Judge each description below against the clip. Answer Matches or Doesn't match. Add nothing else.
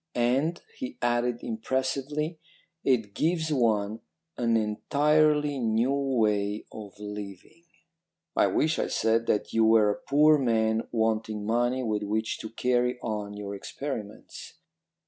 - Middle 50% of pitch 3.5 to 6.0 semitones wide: Matches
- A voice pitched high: Doesn't match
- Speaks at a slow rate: Matches